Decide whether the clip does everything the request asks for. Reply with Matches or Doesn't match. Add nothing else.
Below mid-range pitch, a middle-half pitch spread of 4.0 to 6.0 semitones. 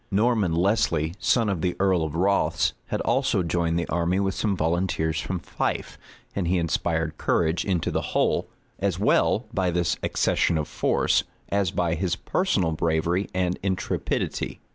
Doesn't match